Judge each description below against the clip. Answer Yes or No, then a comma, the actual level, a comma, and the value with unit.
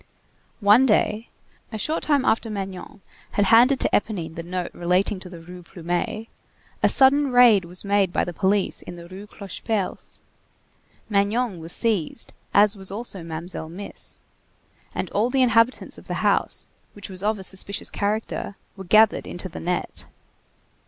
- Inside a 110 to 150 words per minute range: No, average, 160 wpm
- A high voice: Yes, high, 200 Hz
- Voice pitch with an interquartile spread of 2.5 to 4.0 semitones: Yes, average, 3.6 semitones